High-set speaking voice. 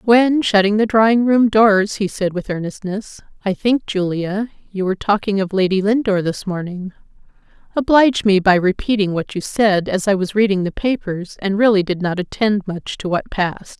Yes: high, 200 Hz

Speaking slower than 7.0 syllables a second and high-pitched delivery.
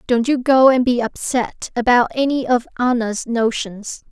Yes: 4.3 syllables/s; high, 240 Hz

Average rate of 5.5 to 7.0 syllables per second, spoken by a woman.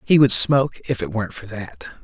No: 5.6 syllables/s; male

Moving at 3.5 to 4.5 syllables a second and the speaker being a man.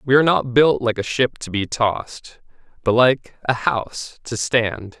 Yes: 4.4 syllables/s; male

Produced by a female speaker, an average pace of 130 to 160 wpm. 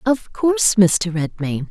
Yes: female; average, 140 wpm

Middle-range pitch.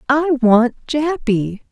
No: very high, 260 Hz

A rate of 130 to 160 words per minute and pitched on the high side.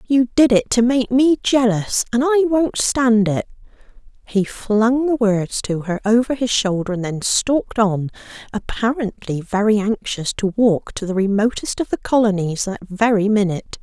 No: average, 170 wpm; high, 220 Hz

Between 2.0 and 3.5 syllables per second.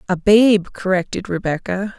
No: 4.6 syllables/s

